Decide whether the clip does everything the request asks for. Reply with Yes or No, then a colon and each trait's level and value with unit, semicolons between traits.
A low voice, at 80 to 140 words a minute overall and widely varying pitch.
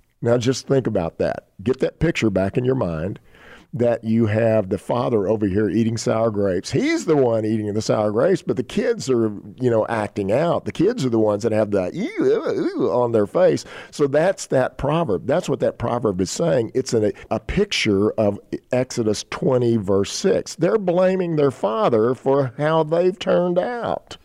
No: low, 120 Hz; average, 195 wpm; wide, 6.9 semitones